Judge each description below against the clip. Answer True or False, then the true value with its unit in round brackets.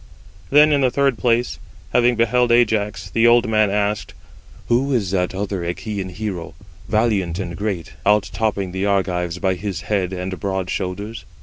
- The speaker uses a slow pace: False (165 wpm)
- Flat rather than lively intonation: False (3.6 semitones)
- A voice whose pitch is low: True (105 Hz)